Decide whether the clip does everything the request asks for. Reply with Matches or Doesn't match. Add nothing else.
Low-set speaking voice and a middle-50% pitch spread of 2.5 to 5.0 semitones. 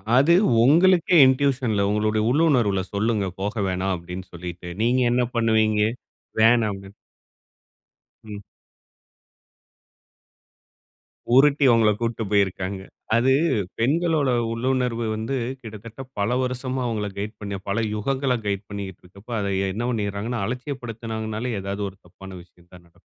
Matches